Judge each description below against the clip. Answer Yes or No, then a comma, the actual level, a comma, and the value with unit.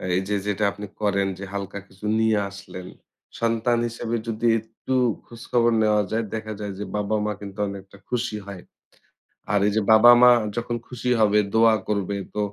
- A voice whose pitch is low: Yes, low, 110 Hz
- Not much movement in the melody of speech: Yes, narrow, 2.2 semitones